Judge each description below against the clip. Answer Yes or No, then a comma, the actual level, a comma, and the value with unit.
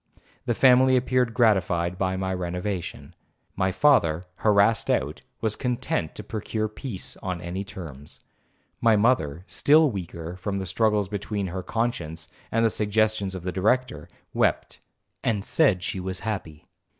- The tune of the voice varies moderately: Yes, average, 3.8 semitones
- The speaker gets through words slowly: No, average, 145 wpm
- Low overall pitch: Yes, low, 100 Hz